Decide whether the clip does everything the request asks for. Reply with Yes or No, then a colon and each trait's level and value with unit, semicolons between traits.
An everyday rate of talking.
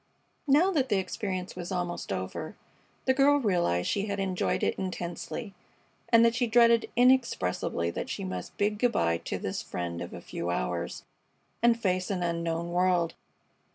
Yes: average, 170 wpm